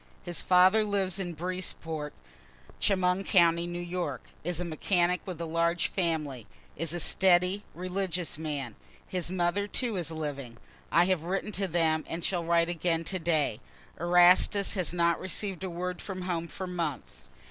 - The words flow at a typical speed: Yes, average, 160 wpm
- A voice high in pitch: No, medium, 175 Hz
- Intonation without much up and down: Yes, narrow, 2.1 semitones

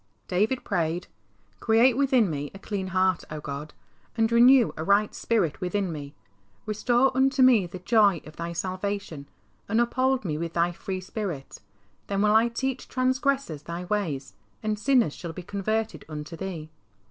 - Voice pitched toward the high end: Yes, high, 200 Hz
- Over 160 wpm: Yes, average, 170 wpm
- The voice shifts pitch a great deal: Yes, wide, 5.7 semitones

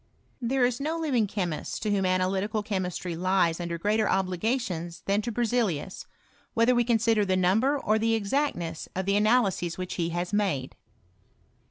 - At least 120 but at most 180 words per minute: Yes, average, 170 wpm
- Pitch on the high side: Yes, high, 200 Hz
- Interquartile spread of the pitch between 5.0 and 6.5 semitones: No, average, 4.1 semitones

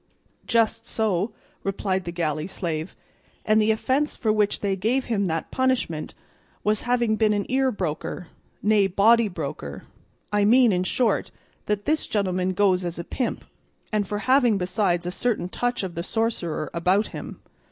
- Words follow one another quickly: No, average, 165 wpm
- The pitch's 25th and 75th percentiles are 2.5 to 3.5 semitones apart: No, average, 4.0 semitones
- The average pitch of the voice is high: Yes, high, 205 Hz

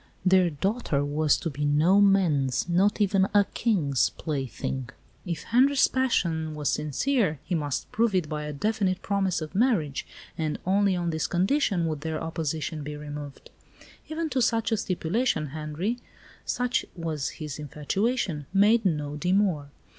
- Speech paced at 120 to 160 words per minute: Yes, average, 150 wpm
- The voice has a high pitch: No, medium, 170 Hz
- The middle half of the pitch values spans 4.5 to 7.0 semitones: Yes, average, 5.2 semitones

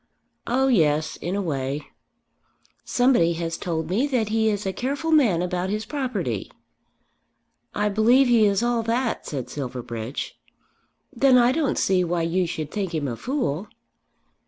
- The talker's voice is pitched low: No, high, 195 Hz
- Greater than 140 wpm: Yes, average, 155 wpm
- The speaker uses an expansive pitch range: Yes, wide, 7.0 semitones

